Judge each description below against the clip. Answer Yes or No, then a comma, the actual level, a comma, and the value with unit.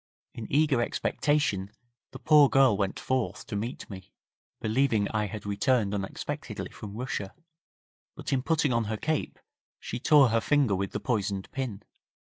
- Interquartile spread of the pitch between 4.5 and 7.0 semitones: Yes, average, 4.9 semitones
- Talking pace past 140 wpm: Yes, average, 155 wpm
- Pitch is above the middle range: No, low, 115 Hz